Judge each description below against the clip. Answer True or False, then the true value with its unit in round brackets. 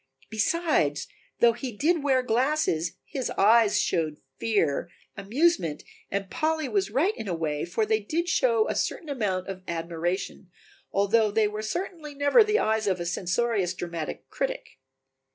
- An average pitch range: False (8.3 semitones)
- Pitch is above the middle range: True (220 Hz)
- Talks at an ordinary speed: True (155 wpm)